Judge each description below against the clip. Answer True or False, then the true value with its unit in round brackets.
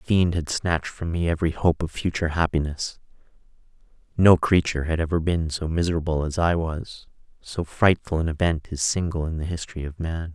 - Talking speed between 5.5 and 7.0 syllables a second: True (5.7 syllables/s)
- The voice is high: False (80 Hz)